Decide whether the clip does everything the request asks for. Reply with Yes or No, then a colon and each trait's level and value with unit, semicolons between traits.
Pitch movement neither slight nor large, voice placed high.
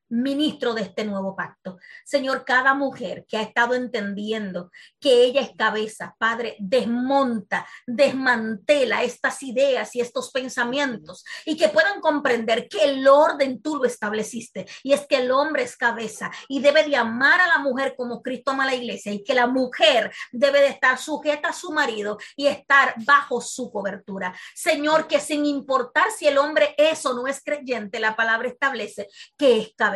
Yes: average, 3.9 semitones; very high, 255 Hz